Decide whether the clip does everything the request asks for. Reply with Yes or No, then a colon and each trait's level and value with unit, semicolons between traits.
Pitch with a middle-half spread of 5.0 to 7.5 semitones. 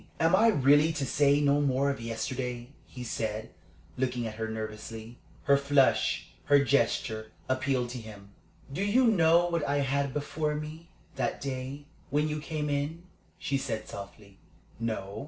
No: average, 4.3 semitones